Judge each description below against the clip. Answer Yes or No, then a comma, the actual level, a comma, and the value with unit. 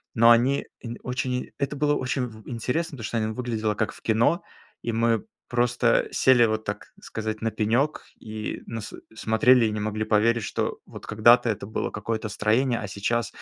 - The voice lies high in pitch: No, low, 115 Hz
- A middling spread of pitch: No, narrow, 2.2 semitones